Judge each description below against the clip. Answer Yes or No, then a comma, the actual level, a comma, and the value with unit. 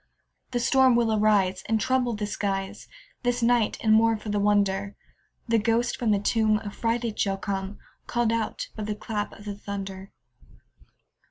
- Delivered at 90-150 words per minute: No, average, 165 wpm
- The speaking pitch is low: No, high, 215 Hz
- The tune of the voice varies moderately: No, narrow, 2.3 semitones